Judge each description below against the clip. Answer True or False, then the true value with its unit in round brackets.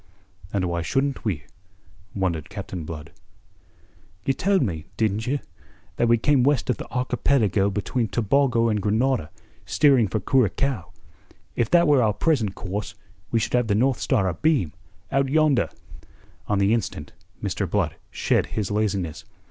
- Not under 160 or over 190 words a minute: False (150 wpm)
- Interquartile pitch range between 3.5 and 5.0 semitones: False (5.4 semitones)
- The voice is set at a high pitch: False (110 Hz)